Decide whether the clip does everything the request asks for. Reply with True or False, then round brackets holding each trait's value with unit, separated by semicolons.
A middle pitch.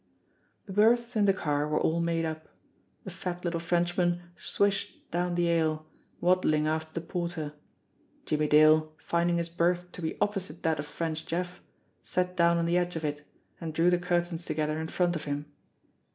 True (170 Hz)